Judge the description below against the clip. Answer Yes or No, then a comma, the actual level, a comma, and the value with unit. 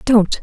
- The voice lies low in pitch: No, high, 225 Hz